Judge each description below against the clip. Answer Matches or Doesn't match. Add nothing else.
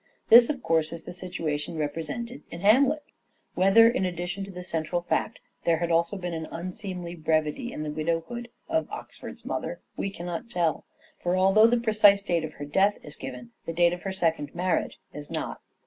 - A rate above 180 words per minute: Matches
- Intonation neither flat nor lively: Matches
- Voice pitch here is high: Doesn't match